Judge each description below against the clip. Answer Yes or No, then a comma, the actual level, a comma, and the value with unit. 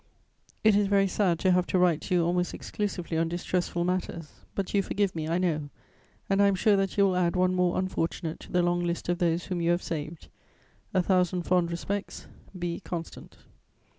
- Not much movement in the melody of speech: Yes, narrow, 1.7 semitones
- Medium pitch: Yes, medium, 180 Hz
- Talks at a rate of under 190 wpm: No, fast, 205 wpm